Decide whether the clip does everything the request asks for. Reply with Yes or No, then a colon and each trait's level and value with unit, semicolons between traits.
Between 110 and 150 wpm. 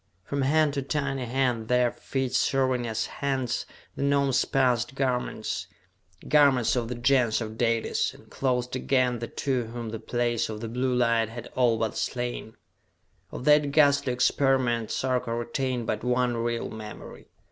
No: average, 160 wpm